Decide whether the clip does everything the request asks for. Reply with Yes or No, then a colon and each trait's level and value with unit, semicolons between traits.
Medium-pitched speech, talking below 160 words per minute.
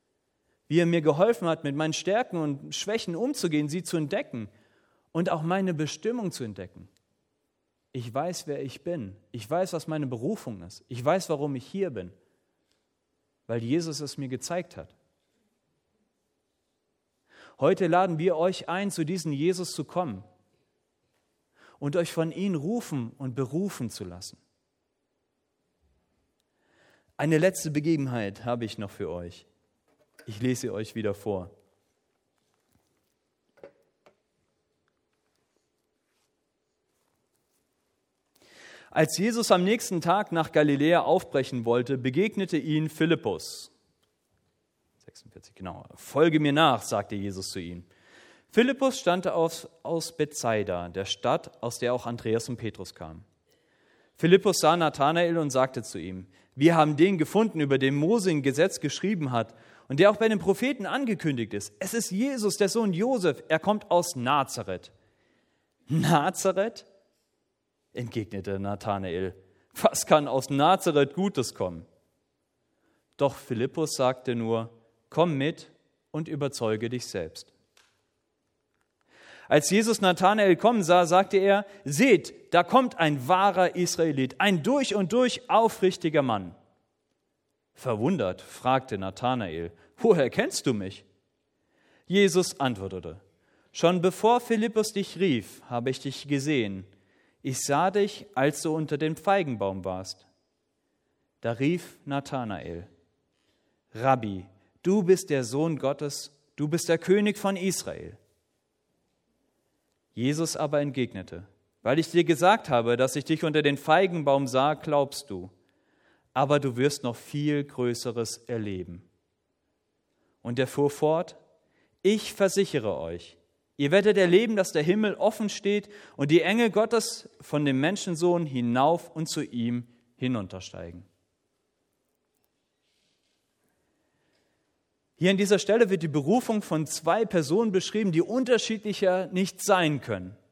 Yes: medium, 150 Hz; slow, 125 wpm